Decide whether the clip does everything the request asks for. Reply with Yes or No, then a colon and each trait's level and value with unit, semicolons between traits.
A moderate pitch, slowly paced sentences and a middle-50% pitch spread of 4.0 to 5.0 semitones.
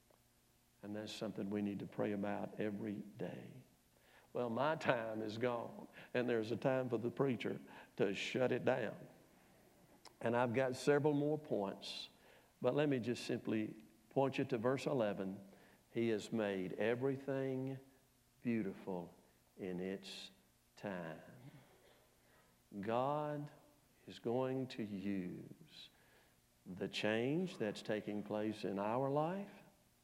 No: low, 115 Hz; slow, 125 wpm; average, 4.6 semitones